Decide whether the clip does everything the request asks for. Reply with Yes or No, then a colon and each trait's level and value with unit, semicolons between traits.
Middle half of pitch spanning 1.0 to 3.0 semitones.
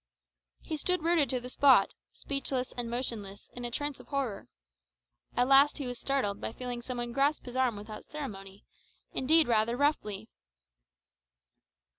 No: average, 3.5 semitones